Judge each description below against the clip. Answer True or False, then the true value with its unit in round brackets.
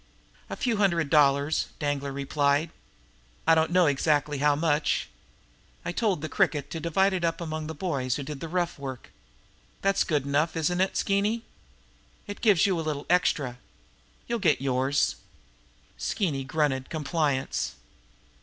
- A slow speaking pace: False (150 wpm)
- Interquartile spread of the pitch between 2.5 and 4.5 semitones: True (3.7 semitones)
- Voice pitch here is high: False (155 Hz)